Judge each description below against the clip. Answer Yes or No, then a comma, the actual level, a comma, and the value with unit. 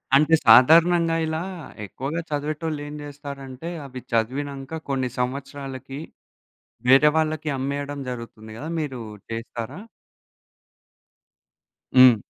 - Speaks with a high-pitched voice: No, medium, 140 Hz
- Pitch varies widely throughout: No, average, 3.0 semitones